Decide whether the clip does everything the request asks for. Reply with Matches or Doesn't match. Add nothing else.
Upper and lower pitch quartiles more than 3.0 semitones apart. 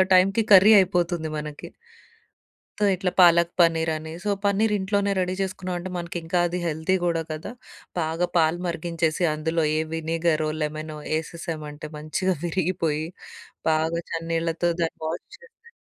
Doesn't match